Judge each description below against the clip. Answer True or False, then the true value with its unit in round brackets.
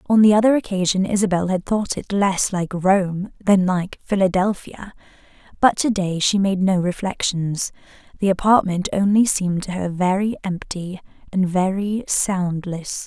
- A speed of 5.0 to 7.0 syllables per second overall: False (4.5 syllables/s)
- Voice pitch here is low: False (190 Hz)